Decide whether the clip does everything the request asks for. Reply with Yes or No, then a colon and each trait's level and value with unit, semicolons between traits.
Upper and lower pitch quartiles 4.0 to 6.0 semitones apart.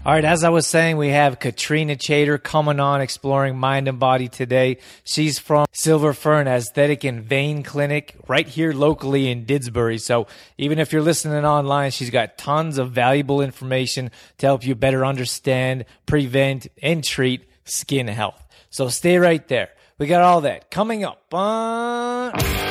No: average, 2.9 semitones